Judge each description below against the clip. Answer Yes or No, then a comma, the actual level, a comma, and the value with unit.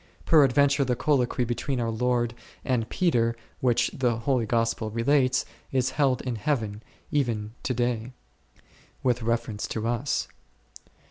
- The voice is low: Yes, low, 120 Hz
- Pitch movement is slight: Yes, narrow, 2.3 semitones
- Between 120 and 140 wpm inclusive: Yes, slow, 135 wpm